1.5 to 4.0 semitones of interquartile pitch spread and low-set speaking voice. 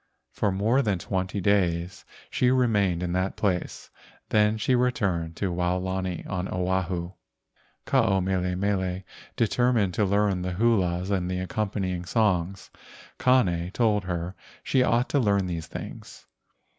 Yes: average, 2.8 semitones; very low, 95 Hz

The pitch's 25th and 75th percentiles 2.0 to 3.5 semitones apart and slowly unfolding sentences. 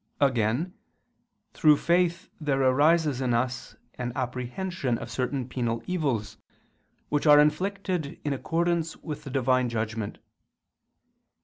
No: average, 4.8 semitones; slow, 115 wpm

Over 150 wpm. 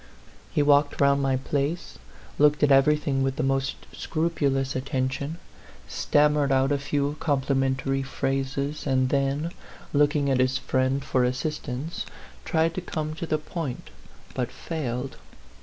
No: slow, 135 wpm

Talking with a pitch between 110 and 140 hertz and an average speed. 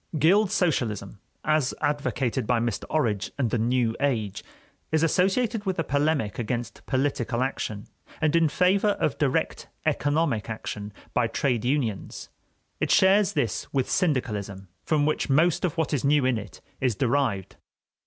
Yes: low, 135 Hz; average, 150 wpm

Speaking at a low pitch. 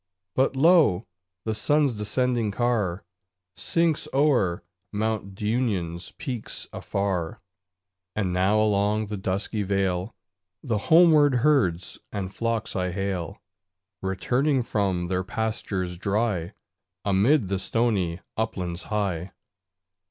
Yes: low, 105 Hz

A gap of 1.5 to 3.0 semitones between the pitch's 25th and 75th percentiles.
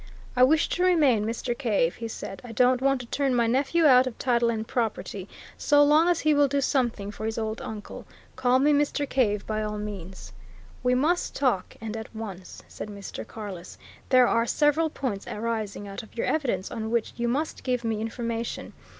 No: average, 4.0 semitones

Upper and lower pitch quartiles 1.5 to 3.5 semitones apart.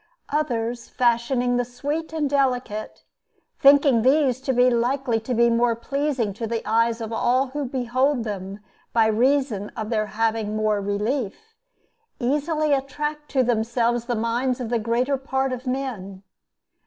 Yes: average, 3.1 semitones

